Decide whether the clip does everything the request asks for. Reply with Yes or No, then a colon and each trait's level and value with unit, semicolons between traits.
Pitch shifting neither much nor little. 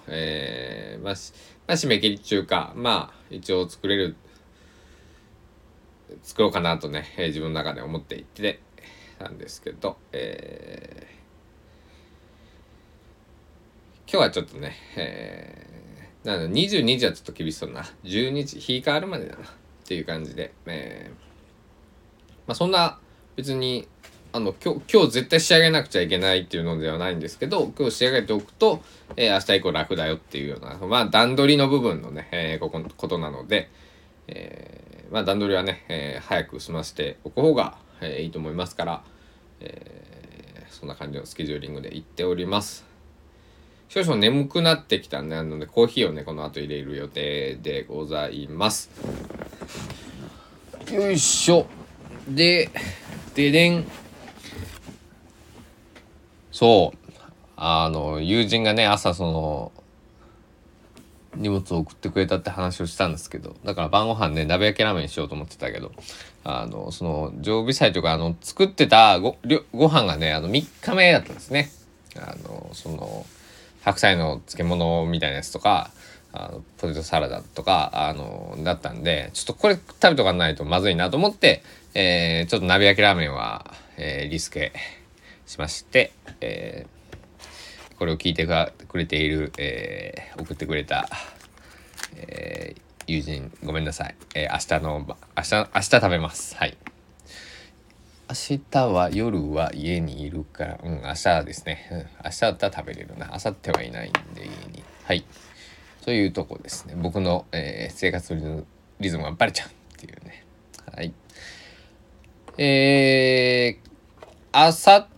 No: wide, 6.4 semitones